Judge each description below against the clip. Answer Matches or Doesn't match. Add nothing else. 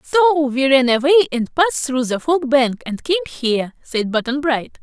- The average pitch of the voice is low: Doesn't match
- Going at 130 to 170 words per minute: Doesn't match